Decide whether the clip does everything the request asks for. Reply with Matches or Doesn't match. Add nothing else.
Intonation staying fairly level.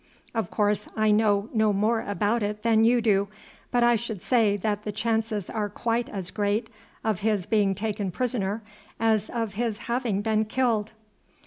Matches